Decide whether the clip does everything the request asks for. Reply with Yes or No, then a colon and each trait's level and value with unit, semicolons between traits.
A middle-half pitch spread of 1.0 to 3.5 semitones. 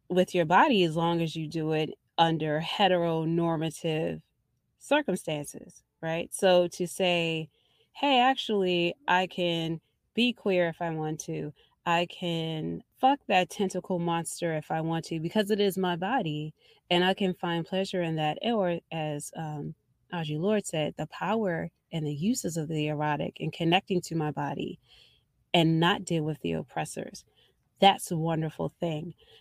Yes: average, 2.8 semitones